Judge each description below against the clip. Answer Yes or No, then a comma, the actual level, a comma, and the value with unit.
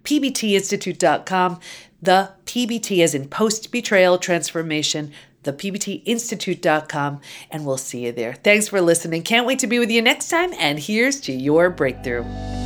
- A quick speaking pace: No, average, 145 wpm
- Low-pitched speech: No, medium, 180 Hz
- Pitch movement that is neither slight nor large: No, wide, 6.6 semitones